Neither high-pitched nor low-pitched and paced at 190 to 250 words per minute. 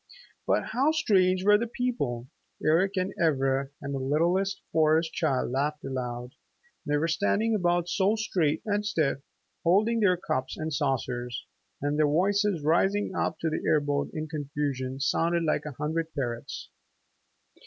No: medium, 160 Hz; average, 155 wpm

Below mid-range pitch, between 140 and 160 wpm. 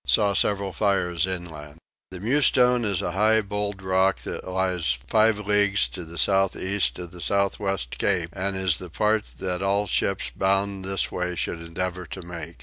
No: very low, 95 Hz; average, 180 wpm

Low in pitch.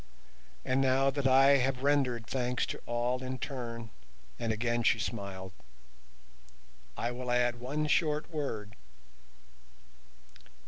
Yes: low, 120 Hz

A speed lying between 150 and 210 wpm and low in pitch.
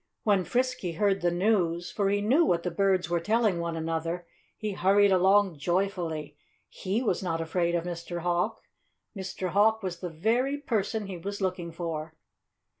No: average, 170 wpm; medium, 185 Hz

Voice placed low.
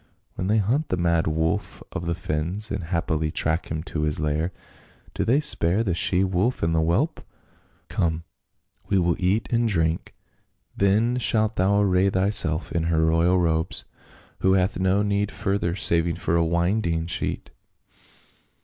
Yes: very low, 90 Hz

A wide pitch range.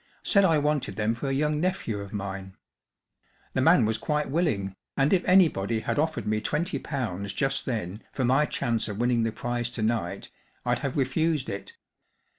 Yes: wide, 5.9 semitones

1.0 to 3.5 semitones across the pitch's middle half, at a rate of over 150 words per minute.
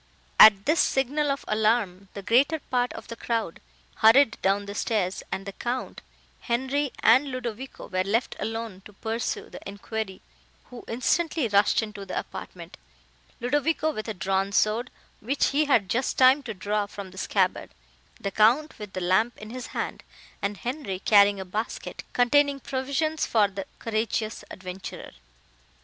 No: average, 4.5 semitones; average, 160 wpm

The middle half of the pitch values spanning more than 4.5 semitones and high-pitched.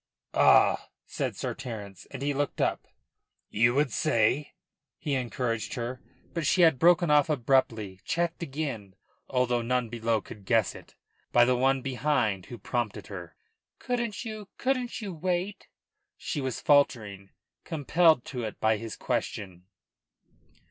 No: wide, 5.6 semitones; low, 125 Hz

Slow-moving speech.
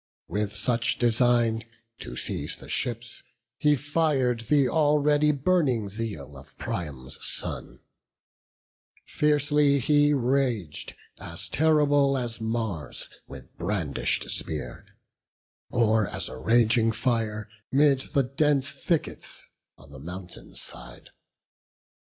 Yes: slow, 105 wpm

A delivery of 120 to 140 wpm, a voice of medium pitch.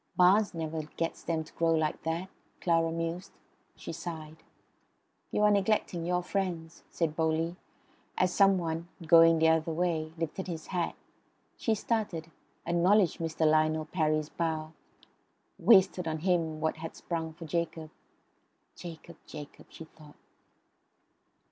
Yes: slow, 135 wpm; medium, 165 Hz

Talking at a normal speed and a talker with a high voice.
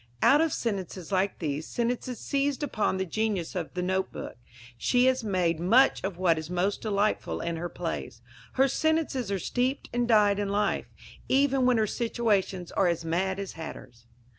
Yes: average, 185 wpm; high, 200 Hz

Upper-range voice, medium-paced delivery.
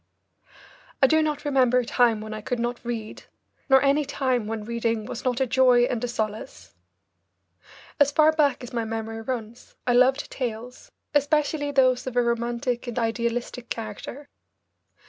Yes: high, 245 Hz; average, 165 wpm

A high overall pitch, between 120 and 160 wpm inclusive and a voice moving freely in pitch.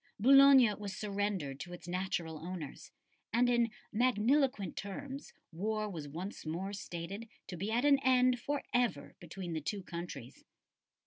Yes: high, 200 Hz; average, 145 wpm; wide, 6.0 semitones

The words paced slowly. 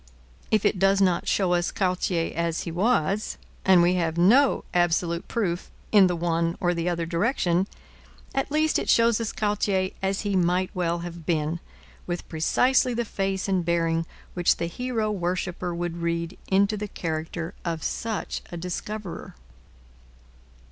No: average, 155 wpm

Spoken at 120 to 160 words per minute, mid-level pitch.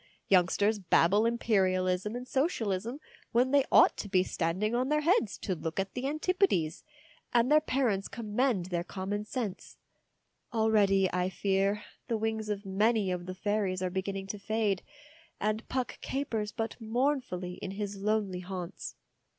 No: average, 150 wpm; high, 210 Hz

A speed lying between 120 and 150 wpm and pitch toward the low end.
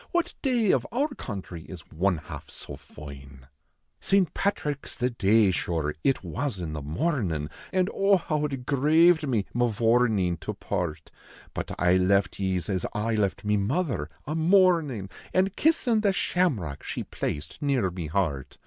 No: average, 165 wpm; low, 110 Hz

